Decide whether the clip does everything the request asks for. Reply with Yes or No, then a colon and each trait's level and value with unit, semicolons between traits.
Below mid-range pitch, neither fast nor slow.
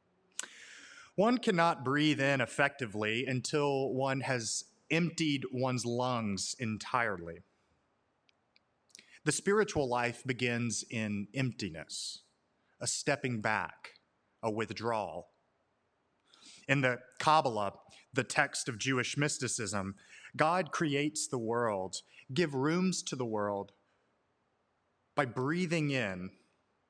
No: low, 130 Hz; slow, 95 wpm